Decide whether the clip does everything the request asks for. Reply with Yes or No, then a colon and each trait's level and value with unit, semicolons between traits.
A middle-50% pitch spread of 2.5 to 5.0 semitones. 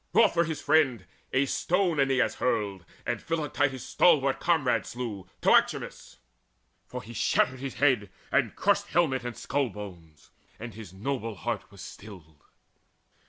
No: wide, 5.6 semitones